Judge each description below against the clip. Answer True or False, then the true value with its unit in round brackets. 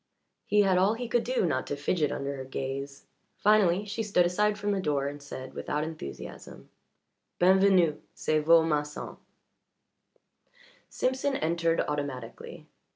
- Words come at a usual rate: True (145 wpm)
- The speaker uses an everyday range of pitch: False (5.9 semitones)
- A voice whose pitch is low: False (165 Hz)